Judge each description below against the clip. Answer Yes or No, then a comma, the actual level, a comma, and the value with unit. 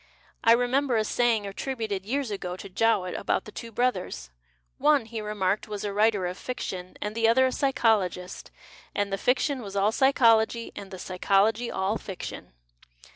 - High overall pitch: Yes, high, 215 Hz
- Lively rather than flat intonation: No, average, 3.6 semitones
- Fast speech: No, average, 175 wpm